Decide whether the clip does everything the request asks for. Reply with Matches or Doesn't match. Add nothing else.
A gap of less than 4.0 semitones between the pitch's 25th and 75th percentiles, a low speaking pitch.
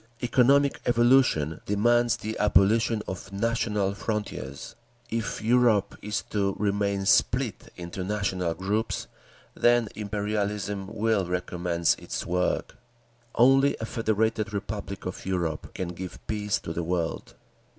Matches